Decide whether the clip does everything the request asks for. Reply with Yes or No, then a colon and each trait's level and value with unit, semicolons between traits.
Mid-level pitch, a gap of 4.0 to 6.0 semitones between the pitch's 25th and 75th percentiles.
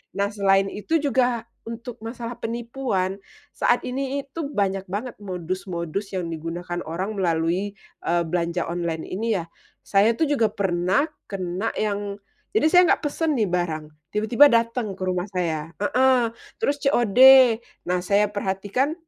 No: high, 200 Hz; average, 4.7 semitones